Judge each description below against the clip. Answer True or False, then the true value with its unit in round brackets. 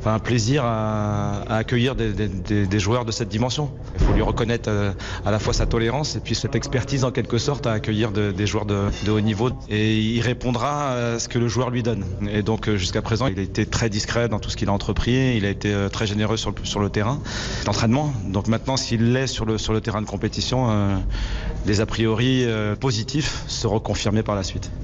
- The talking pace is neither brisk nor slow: False (235 wpm)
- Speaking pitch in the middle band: False (110 Hz)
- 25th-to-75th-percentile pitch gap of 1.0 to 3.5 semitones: True (2.5 semitones)